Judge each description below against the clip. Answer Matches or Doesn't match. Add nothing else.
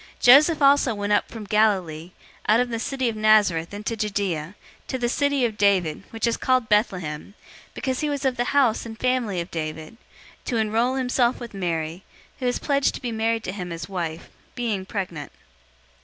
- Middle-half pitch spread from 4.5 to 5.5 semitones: Matches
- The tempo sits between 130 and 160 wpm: Doesn't match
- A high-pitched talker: Matches